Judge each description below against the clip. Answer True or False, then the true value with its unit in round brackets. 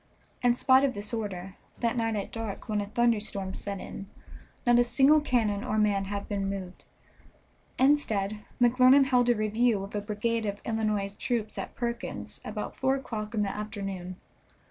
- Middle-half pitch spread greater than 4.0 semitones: False (3.1 semitones)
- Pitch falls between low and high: False (215 Hz)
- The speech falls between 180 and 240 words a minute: False (170 wpm)